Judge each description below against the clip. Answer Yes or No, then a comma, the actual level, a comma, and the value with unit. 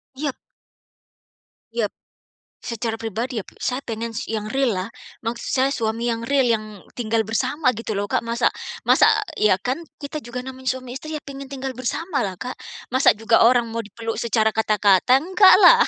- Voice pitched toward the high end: Yes, high, 235 Hz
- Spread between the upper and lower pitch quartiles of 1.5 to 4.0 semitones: Yes, average, 3.1 semitones